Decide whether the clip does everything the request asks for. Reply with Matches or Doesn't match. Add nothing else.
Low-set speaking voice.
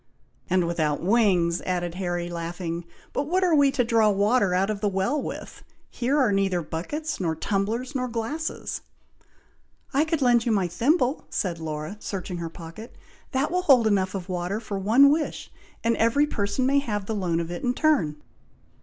Doesn't match